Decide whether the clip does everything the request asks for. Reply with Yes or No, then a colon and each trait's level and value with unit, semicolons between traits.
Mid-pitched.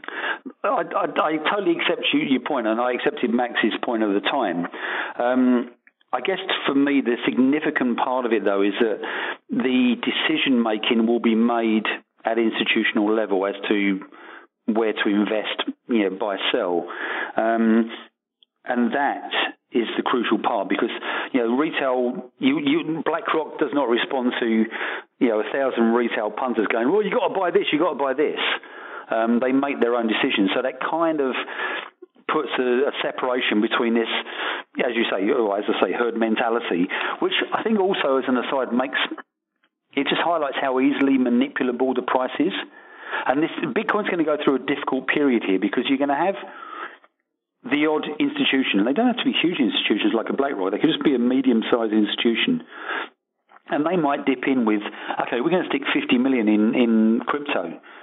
No: low, 130 Hz